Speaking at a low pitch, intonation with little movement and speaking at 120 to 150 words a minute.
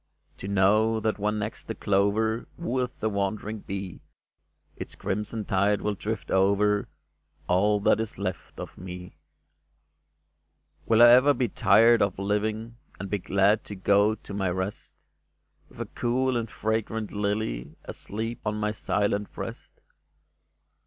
Yes: low, 105 Hz; narrow, 1.9 semitones; average, 140 wpm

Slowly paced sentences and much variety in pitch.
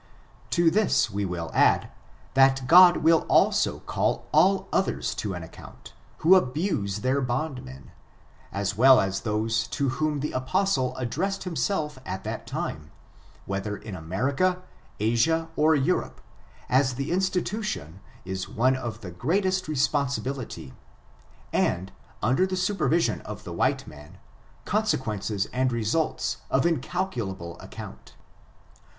Yes: slow, 130 wpm; wide, 8.2 semitones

